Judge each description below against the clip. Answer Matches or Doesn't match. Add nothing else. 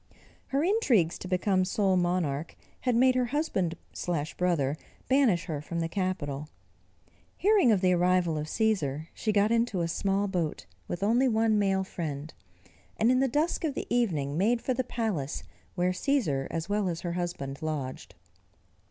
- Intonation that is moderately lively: Doesn't match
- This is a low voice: Doesn't match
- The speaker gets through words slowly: Doesn't match